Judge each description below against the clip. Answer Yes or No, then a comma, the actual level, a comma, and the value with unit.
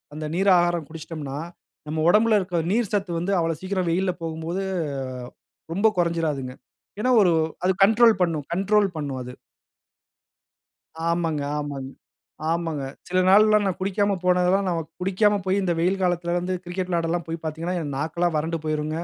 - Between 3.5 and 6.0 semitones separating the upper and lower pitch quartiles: No, average, 3.1 semitones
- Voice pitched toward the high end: No, medium, 175 Hz